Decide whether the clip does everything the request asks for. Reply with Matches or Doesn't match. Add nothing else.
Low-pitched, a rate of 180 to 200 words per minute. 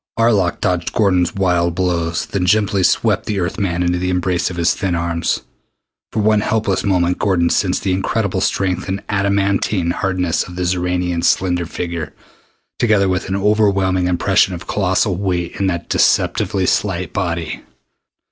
Doesn't match